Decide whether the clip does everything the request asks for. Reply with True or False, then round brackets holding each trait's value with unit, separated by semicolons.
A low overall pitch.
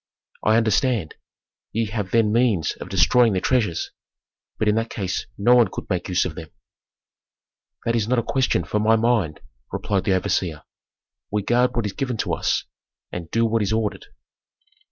True (110 Hz)